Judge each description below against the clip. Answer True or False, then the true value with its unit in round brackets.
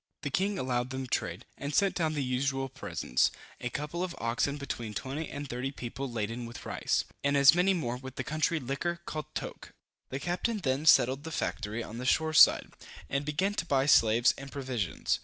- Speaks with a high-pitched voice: False (135 Hz)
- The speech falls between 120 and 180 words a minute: False (195 wpm)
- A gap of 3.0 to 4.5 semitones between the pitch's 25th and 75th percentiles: True (4.0 semitones)